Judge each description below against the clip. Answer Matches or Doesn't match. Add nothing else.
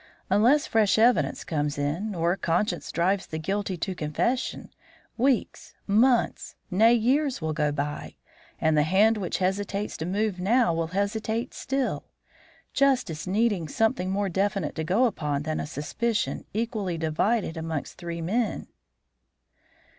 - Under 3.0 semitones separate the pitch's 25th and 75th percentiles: Doesn't match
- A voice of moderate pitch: Doesn't match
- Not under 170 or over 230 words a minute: Doesn't match